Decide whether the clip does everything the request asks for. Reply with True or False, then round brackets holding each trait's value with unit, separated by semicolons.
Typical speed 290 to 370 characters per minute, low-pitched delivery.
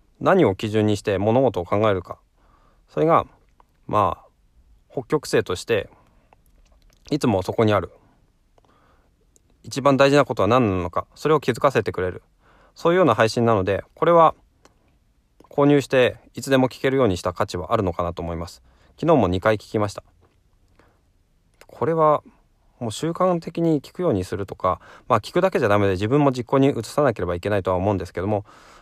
True (340 characters per minute; 110 Hz)